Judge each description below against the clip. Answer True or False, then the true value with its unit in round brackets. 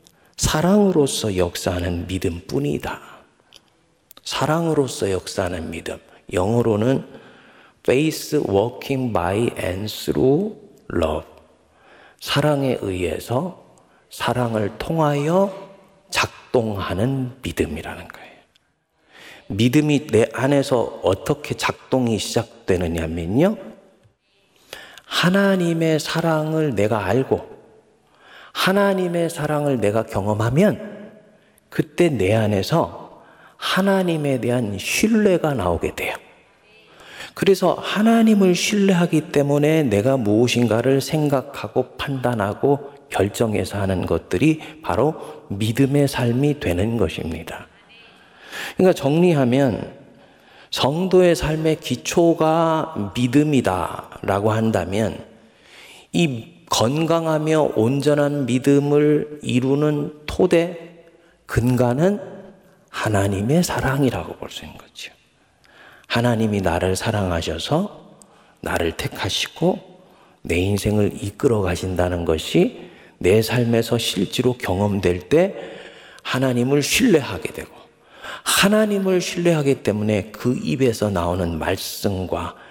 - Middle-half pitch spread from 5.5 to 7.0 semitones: False (7.4 semitones)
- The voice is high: False (130 Hz)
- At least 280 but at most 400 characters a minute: False (235 characters per minute)